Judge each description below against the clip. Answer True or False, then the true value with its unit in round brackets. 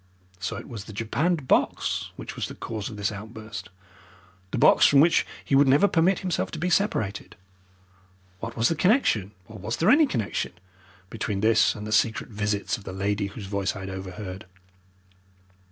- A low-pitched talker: True (110 Hz)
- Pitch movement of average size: False (5.9 semitones)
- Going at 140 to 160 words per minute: False (185 wpm)